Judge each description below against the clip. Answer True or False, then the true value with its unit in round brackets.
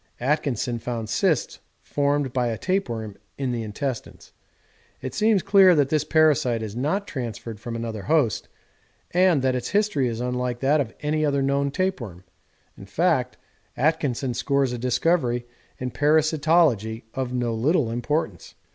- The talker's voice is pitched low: True (130 Hz)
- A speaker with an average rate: True (145 wpm)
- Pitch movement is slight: False (4.4 semitones)